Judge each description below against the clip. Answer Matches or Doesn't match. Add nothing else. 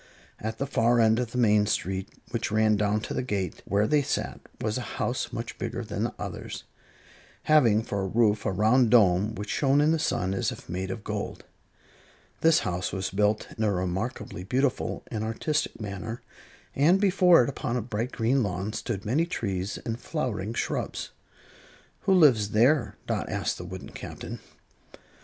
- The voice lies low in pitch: Matches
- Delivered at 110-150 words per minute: Doesn't match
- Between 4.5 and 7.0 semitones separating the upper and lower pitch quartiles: Doesn't match